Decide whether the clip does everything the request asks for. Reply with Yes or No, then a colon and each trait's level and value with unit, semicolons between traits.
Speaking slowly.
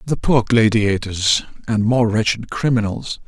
Yes: slow, 130 wpm